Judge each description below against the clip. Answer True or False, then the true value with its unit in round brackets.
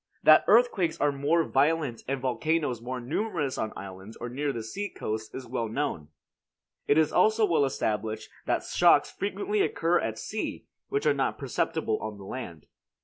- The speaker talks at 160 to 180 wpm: True (170 wpm)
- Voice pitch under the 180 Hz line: True (140 Hz)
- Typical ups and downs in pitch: False (6.6 semitones)